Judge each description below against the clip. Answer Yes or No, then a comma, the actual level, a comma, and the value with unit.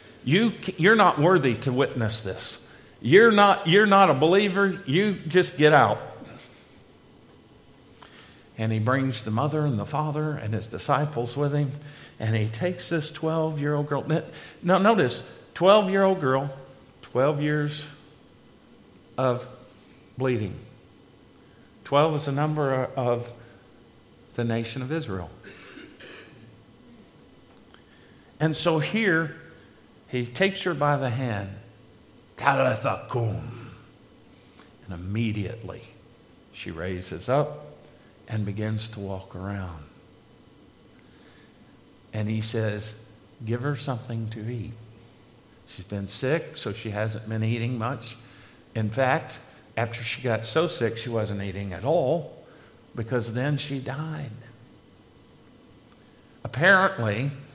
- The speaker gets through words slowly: Yes, slow, 110 wpm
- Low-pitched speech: Yes, low, 125 Hz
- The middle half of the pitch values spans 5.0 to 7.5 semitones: Yes, average, 5.3 semitones